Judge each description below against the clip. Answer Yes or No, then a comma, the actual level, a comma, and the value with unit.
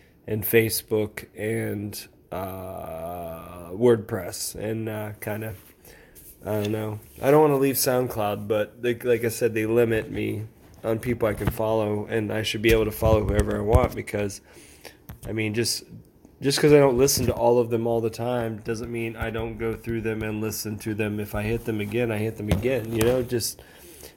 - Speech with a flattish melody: Yes, narrow, 1.8 semitones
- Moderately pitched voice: No, low, 110 Hz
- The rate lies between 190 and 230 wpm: Yes, average, 200 wpm